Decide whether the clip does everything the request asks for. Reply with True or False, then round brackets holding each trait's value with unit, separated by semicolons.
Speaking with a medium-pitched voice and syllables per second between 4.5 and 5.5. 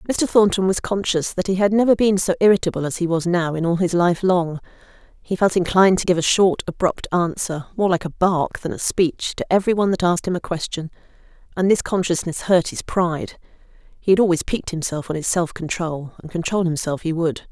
False (175 Hz; 5.8 syllables/s)